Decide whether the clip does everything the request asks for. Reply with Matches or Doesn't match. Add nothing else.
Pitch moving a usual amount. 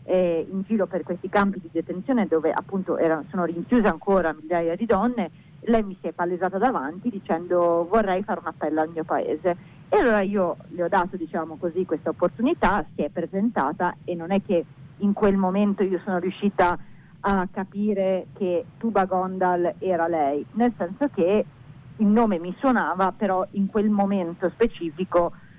Matches